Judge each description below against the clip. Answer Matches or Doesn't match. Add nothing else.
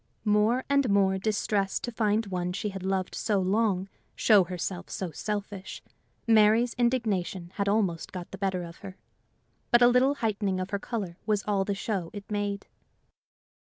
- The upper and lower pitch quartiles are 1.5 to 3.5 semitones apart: Matches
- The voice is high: Matches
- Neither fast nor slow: Matches